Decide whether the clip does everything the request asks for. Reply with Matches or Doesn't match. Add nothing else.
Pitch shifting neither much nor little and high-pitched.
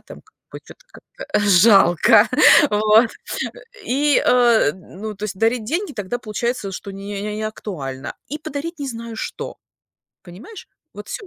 Matches